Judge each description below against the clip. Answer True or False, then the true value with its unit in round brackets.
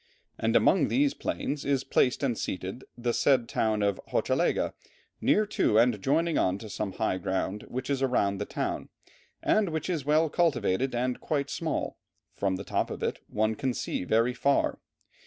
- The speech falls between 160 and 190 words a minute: True (175 wpm)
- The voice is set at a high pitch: False (125 Hz)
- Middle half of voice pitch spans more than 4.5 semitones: True (5.5 semitones)